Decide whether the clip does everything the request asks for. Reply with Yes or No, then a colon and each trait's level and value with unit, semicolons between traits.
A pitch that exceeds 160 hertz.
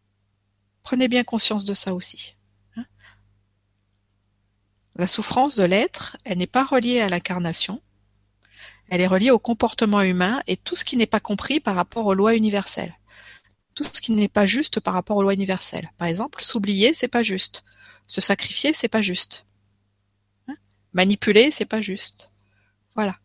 Yes: high, 190 Hz